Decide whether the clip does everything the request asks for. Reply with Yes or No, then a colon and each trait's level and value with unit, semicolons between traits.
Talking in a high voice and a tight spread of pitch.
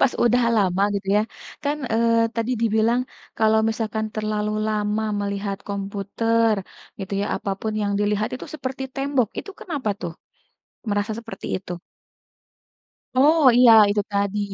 Yes: high, 215 Hz; narrow, 2.3 semitones